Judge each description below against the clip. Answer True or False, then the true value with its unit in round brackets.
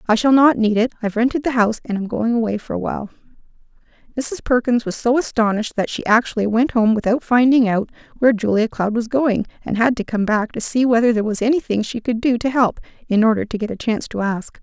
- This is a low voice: False (230 Hz)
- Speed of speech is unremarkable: False (240 wpm)